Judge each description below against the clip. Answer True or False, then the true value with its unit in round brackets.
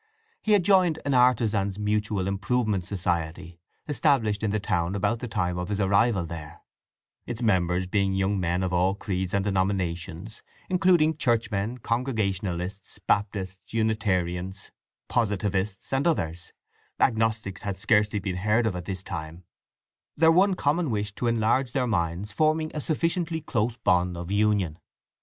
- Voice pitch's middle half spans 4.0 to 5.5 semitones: True (4.3 semitones)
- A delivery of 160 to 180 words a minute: False (140 wpm)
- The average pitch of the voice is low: True (105 Hz)